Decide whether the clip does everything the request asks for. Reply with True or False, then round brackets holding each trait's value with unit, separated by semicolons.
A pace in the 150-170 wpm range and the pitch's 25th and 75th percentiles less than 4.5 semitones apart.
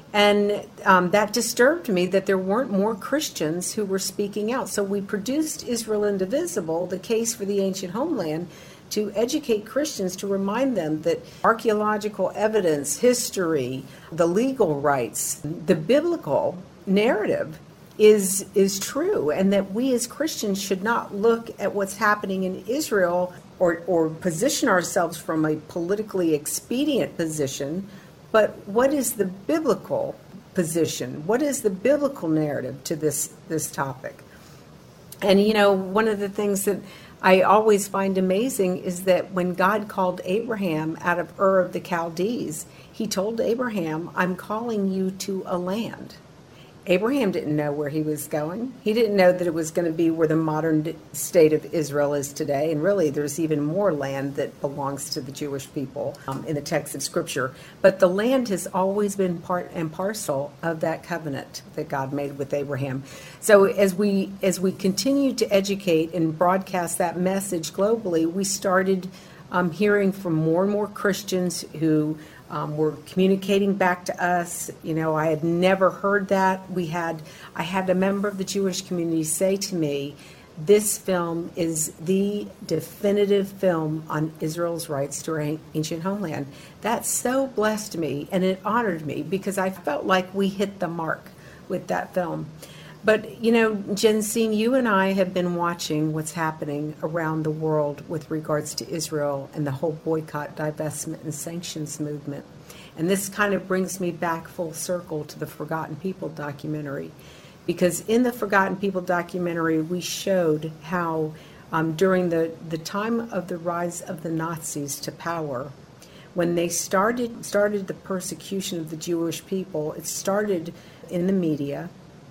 True (160 wpm; 4.0 semitones)